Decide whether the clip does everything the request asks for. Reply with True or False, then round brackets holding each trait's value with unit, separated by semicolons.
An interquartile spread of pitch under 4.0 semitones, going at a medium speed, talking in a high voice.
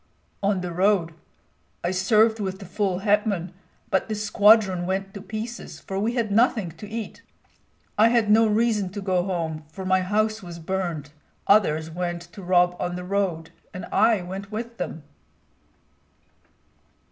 True (3.2 semitones; 160 wpm; 195 Hz)